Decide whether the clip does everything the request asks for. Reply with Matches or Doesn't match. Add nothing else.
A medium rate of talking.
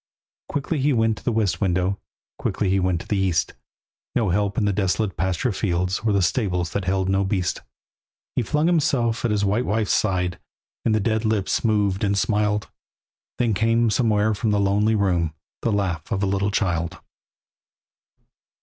Matches